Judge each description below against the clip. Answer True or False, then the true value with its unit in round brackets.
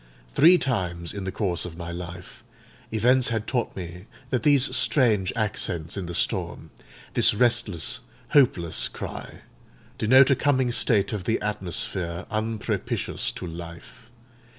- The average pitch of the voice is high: False (105 Hz)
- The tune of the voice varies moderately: False (5.8 semitones)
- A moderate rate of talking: False (130 wpm)